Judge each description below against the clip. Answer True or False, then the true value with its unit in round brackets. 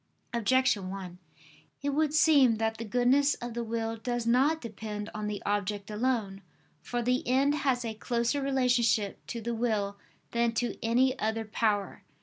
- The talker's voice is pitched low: False (235 Hz)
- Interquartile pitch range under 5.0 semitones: True (3.1 semitones)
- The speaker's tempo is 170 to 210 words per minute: False (160 wpm)